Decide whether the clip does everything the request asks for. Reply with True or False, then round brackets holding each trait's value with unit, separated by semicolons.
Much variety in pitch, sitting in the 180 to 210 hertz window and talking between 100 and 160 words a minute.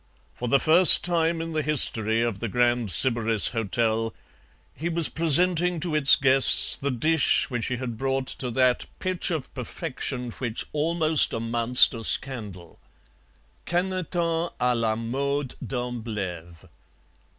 False (5.7 semitones; 130 Hz; 135 wpm)